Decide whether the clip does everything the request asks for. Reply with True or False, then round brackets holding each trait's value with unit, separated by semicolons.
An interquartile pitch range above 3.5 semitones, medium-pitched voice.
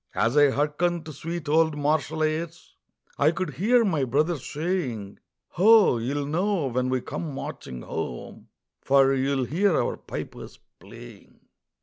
True (4.1 semitones; 150 Hz)